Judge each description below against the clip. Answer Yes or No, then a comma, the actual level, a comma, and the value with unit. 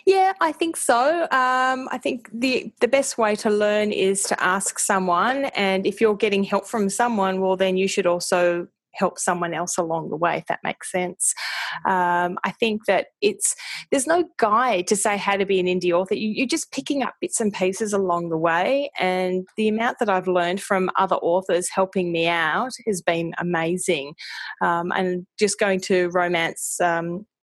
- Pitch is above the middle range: Yes, high, 195 Hz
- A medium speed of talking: Yes, average, 190 wpm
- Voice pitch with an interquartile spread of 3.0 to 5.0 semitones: Yes, average, 4.6 semitones